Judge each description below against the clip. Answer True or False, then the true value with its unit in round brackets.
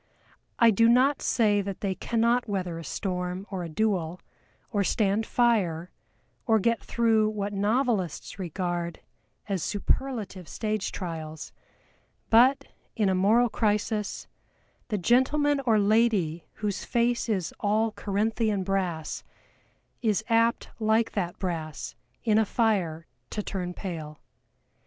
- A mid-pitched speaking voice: False (205 Hz)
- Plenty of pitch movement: False (3.9 semitones)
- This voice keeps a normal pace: False (125 wpm)